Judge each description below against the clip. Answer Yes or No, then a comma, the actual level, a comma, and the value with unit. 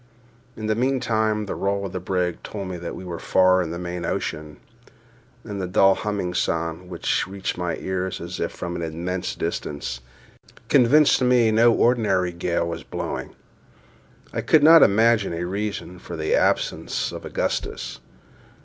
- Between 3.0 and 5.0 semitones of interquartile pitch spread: Yes, average, 3.8 semitones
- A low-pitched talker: Yes, very low, 95 Hz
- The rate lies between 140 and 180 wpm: Yes, average, 165 wpm